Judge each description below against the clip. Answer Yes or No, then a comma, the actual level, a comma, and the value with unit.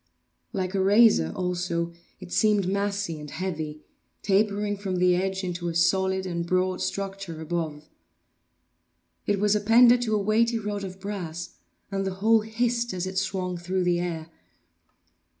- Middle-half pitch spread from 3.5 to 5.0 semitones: No, narrow, 2.6 semitones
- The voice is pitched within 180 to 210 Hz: Yes, high, 190 Hz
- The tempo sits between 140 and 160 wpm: Yes, average, 150 wpm